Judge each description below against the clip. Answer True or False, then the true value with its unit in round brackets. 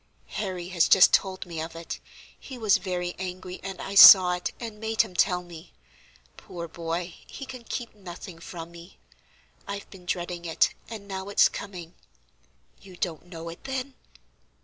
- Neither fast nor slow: True (170 wpm)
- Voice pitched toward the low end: False (180 Hz)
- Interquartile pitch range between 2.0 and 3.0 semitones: True (2.7 semitones)